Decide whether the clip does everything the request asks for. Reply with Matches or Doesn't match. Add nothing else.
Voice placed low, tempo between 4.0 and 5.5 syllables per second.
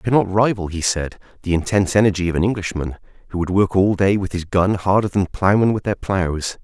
Doesn't match